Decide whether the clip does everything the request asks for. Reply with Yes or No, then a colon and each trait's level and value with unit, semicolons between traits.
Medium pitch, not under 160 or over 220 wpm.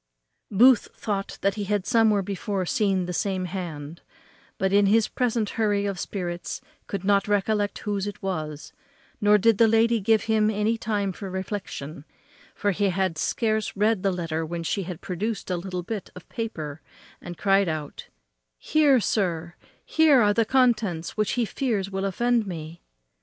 No: high, 200 Hz; average, 165 wpm